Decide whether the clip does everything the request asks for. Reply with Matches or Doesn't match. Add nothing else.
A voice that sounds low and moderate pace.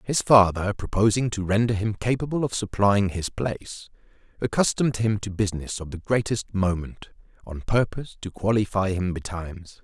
Matches